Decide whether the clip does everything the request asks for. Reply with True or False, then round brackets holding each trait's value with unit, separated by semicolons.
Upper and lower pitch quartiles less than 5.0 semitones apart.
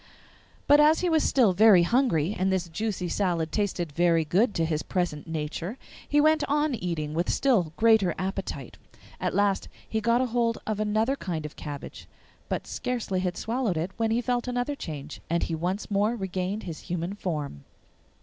False (5.5 semitones)